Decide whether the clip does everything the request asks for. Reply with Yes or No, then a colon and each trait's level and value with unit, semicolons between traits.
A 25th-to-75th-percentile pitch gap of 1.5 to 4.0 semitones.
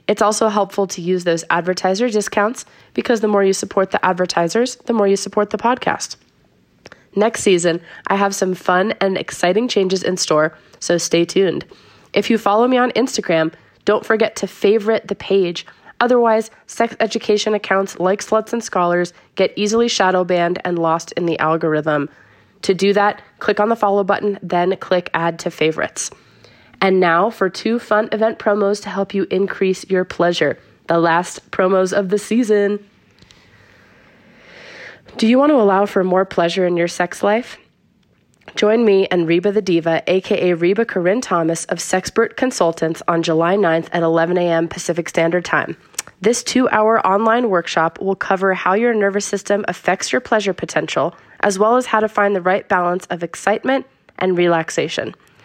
Yes: average, 3.4 semitones